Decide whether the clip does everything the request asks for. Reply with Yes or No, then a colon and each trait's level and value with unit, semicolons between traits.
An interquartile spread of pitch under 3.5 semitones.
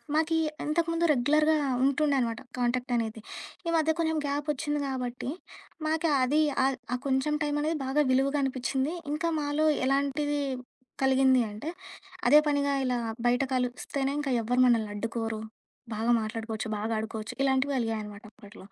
No: average, 3.8 semitones